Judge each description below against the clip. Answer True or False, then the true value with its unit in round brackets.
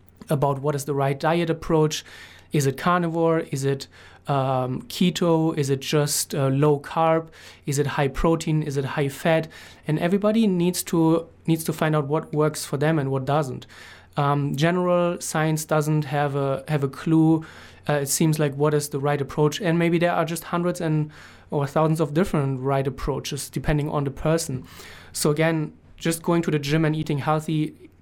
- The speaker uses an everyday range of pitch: False (2.3 semitones)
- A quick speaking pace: False (190 wpm)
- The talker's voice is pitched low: False (155 Hz)